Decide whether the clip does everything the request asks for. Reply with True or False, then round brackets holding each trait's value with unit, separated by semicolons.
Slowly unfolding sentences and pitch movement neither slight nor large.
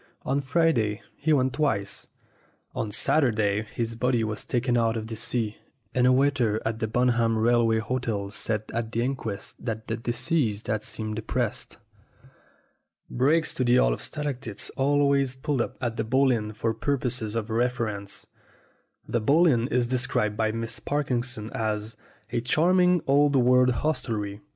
False (160 wpm; 3.1 semitones)